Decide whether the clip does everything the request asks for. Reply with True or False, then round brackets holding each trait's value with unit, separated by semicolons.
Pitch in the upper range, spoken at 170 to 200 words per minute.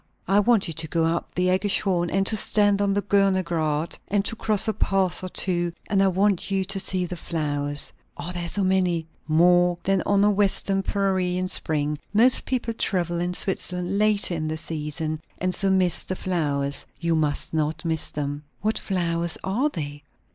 False (180 Hz; 190 wpm)